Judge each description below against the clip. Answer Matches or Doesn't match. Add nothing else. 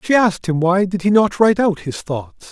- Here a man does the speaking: Matches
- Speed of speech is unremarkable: Doesn't match